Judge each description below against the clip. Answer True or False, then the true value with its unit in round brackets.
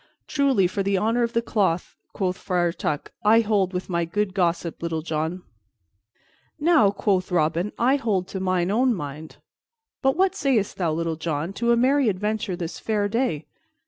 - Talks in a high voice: True (195 Hz)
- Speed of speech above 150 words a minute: True (175 wpm)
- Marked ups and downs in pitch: False (5.0 semitones)